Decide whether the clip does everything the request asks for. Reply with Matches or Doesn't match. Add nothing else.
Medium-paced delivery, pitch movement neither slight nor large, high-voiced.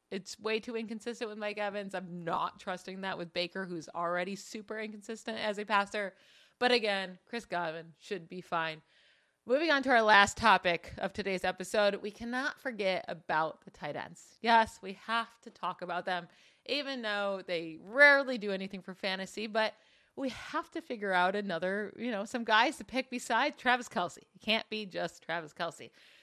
Matches